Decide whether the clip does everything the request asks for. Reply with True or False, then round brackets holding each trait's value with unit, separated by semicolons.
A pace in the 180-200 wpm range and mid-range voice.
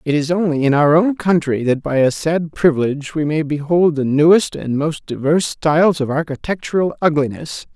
True (185 wpm; 155 Hz)